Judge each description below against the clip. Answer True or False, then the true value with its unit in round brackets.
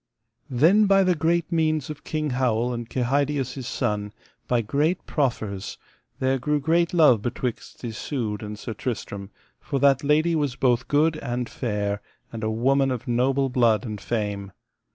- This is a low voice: True (130 Hz)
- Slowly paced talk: False (160 wpm)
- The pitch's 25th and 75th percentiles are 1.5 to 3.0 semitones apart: False (4.7 semitones)